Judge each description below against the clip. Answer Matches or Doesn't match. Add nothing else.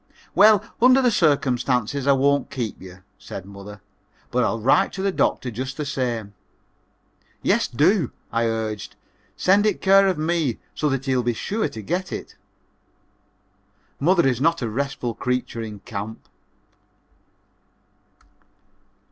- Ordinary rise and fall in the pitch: Doesn't match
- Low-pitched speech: Matches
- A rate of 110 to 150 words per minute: Matches